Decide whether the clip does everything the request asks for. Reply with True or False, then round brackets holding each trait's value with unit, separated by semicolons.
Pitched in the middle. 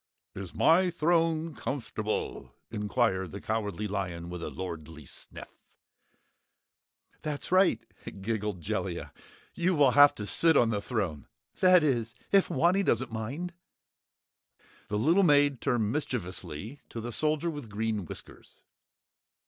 False (115 Hz)